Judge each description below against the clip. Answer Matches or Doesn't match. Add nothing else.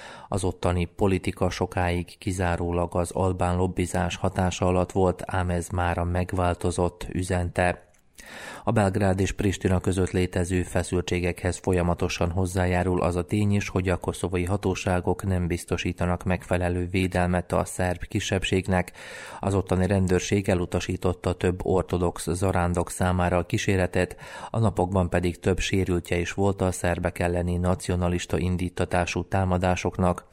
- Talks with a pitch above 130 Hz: Doesn't match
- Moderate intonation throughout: Doesn't match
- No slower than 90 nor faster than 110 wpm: Doesn't match